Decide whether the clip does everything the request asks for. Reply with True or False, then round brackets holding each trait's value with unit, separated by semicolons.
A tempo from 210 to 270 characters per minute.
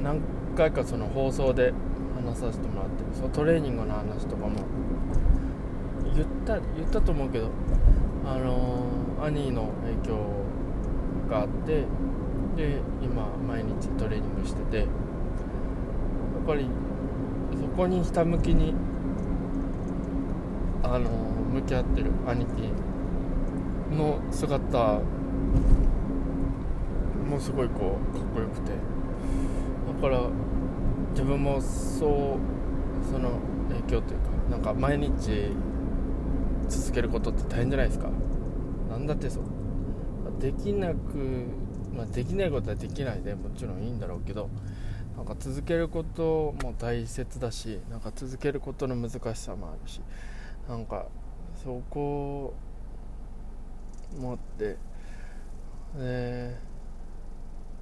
True (220 characters per minute)